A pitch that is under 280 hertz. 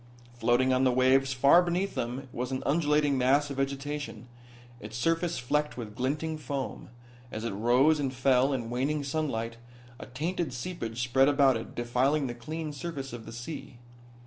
Yes: low, 135 Hz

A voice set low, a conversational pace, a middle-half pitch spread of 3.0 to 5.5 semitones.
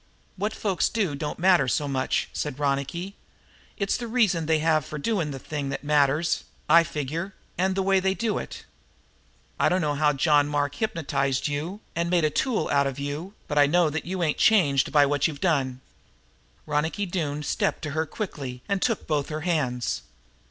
No: medium, 155 Hz; average, 190 wpm; average, 4.3 semitones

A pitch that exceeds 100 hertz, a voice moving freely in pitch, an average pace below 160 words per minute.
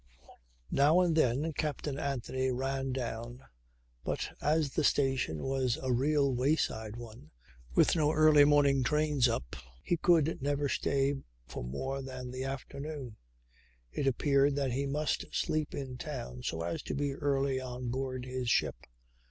No: low, 135 Hz; narrow, 2.4 semitones; average, 150 wpm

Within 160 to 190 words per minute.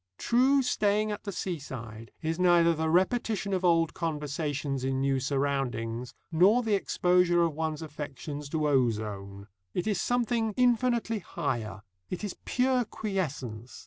No: average, 140 wpm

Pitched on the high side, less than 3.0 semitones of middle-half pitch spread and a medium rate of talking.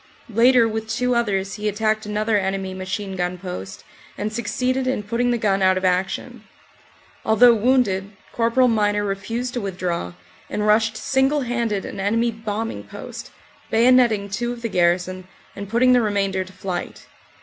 No: high, 210 Hz; average, 3.5 semitones; average, 165 wpm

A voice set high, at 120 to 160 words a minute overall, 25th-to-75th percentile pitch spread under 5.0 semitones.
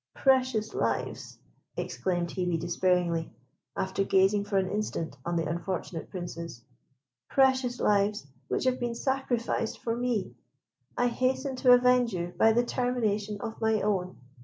No: high, 210 Hz; slow, 135 wpm; wide, 5.4 semitones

